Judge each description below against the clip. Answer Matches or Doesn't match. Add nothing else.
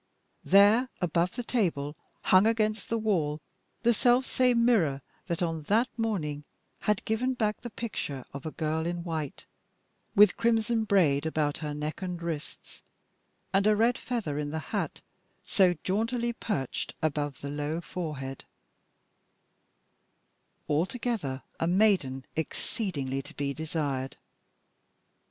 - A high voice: Doesn't match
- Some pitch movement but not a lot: Doesn't match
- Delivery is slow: Matches